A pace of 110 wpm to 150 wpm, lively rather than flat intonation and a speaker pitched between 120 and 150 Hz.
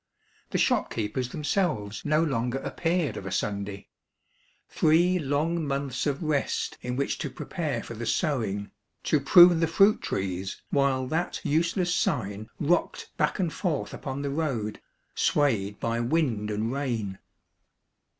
Yes: average, 140 wpm; wide, 6.5 semitones; medium, 140 Hz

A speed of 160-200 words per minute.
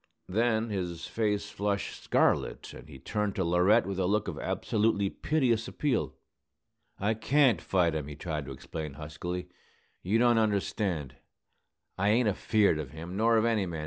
Yes: average, 165 wpm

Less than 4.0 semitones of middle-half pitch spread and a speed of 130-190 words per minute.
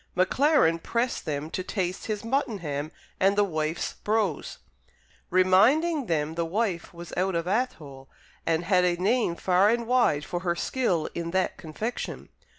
No: average, 5.2 semitones; average, 155 wpm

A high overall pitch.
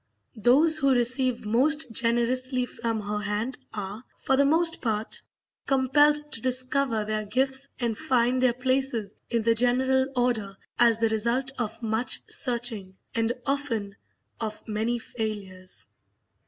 Yes: high, 240 Hz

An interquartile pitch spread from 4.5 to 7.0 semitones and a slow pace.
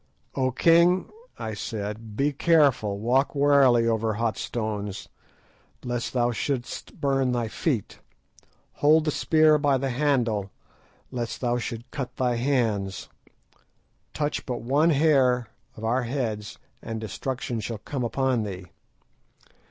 No: average, 3.9 semitones; slow, 130 wpm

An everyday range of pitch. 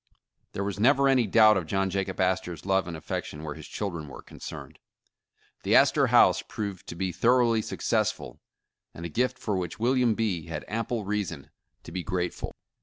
Yes: average, 4.5 semitones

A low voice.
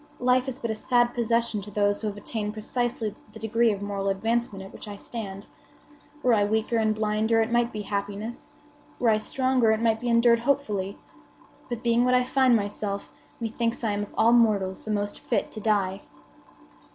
No: high, 220 Hz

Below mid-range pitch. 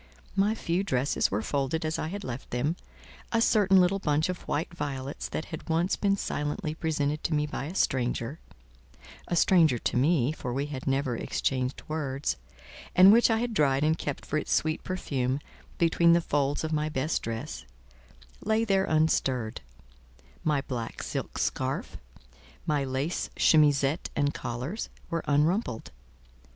No: medium, 150 Hz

